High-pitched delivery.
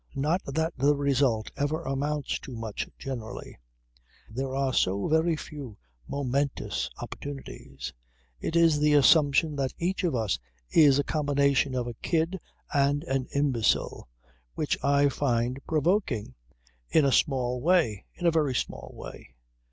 No: medium, 140 Hz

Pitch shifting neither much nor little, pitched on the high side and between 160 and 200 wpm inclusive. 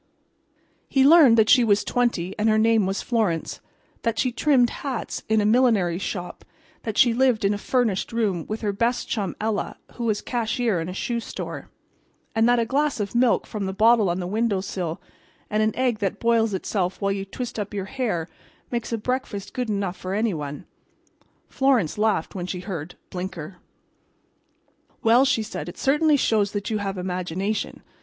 Yes: average, 3.6 semitones; high, 215 Hz; average, 185 wpm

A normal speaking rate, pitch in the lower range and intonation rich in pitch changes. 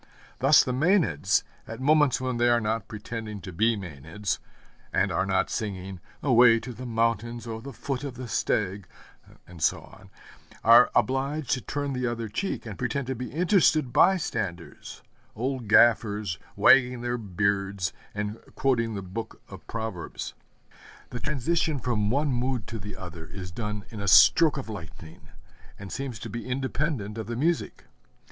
No: average, 165 wpm; low, 115 Hz; average, 4.3 semitones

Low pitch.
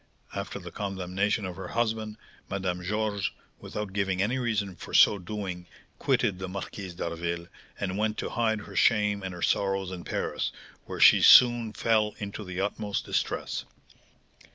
Yes: low, 100 Hz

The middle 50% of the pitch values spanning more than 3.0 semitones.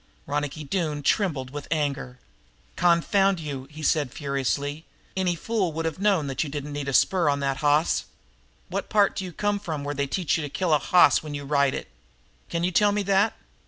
Yes: average, 4.2 semitones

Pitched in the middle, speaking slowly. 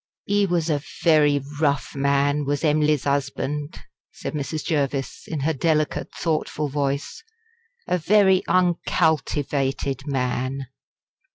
Yes: medium, 145 Hz; slow, 110 wpm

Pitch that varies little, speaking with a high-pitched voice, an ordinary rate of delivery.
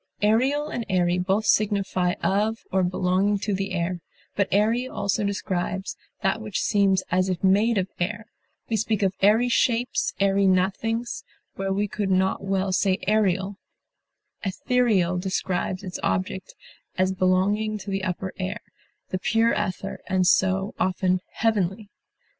Yes: narrow, 2.3 semitones; high, 195 Hz; average, 145 wpm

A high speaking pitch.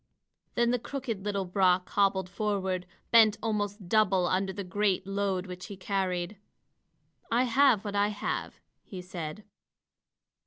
Yes: high, 200 Hz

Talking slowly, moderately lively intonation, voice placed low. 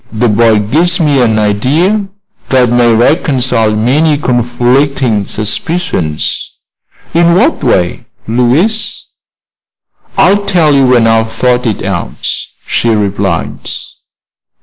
No: slow, 105 wpm; wide, 5.7 semitones; low, 125 Hz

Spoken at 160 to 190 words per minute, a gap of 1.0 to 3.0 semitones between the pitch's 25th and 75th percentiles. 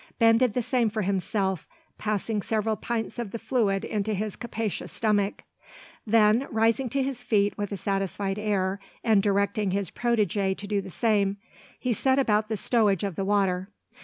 Yes: average, 175 wpm; narrow, 2.4 semitones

